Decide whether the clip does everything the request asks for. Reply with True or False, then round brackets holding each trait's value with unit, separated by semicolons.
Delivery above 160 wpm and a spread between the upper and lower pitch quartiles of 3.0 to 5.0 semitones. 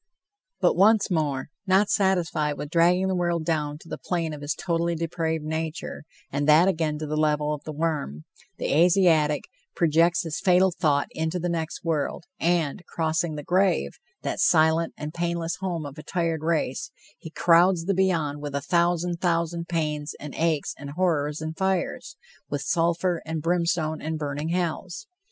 False (170 wpm; 2.4 semitones)